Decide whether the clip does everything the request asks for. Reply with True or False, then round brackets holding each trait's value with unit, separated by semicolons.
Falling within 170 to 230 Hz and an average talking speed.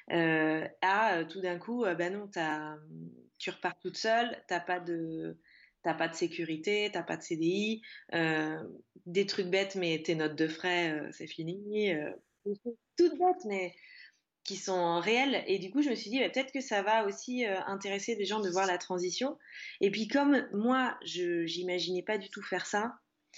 True (185 Hz; 185 wpm)